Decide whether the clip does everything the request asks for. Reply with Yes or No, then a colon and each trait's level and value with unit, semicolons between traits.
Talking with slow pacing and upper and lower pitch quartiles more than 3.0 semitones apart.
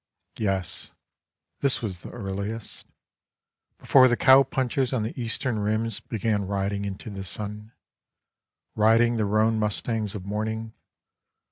No: slow, 125 wpm; narrow, 2.4 semitones